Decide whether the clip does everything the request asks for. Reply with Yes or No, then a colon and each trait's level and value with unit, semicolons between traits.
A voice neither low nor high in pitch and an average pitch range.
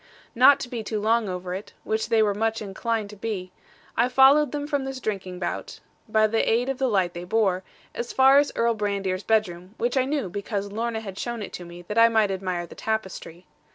No: high, 220 Hz; average, 3.7 semitones